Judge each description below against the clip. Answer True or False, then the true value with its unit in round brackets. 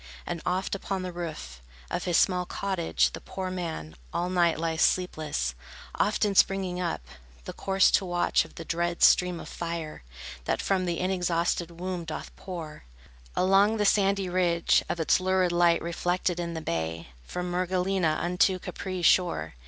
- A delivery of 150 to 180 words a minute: True (160 wpm)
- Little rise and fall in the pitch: True (1.9 semitones)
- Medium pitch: True (175 Hz)